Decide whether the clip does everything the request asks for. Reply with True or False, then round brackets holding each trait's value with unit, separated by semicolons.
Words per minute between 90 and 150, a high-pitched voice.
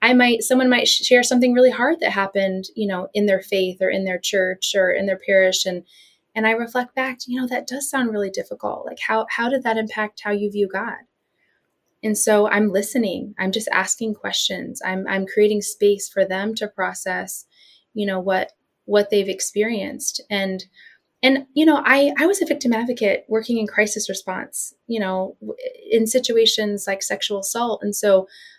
False (190 wpm; 210 Hz)